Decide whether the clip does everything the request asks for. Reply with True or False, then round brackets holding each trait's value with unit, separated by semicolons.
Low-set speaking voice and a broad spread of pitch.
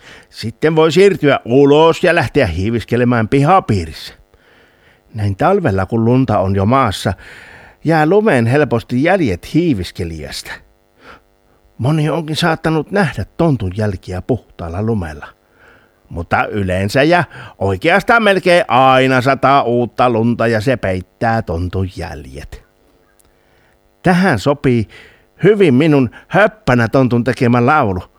True (120 Hz; 7.6 semitones)